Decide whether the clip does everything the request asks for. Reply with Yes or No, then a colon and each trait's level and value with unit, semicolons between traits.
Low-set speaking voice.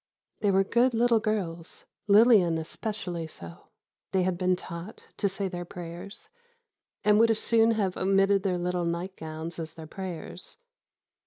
No: medium, 185 Hz